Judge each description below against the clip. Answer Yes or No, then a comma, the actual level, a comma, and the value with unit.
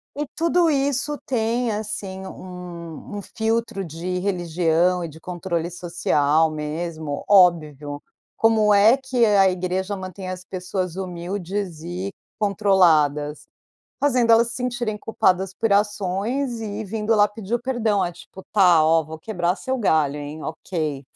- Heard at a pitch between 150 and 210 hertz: Yes, high, 190 Hz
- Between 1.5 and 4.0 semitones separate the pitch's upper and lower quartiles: No, average, 4.4 semitones